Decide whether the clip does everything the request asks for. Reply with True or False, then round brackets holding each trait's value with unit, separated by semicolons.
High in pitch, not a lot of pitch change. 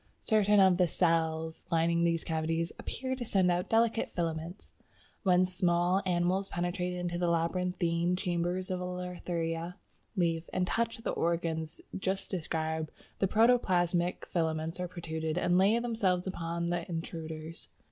False (175 Hz; 1.9 semitones)